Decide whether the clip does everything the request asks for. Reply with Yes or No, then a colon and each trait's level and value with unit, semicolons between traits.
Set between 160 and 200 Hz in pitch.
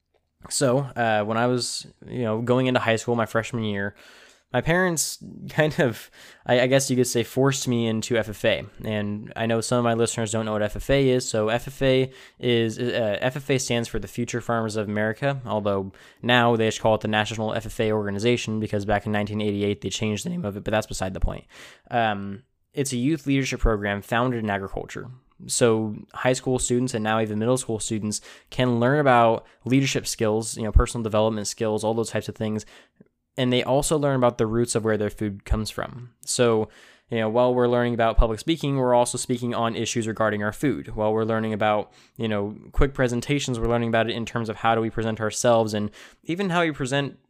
No: low, 115 Hz